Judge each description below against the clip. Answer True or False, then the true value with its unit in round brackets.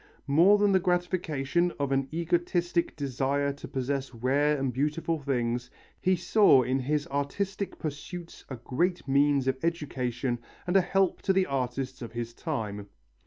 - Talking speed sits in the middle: True (155 wpm)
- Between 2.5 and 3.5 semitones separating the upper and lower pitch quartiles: False (4.9 semitones)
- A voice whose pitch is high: False (140 Hz)